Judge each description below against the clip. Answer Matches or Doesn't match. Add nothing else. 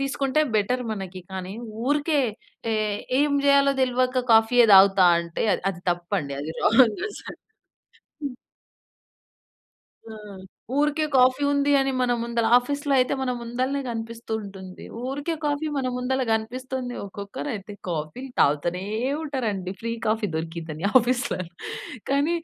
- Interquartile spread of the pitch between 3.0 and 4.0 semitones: Doesn't match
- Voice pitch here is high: Matches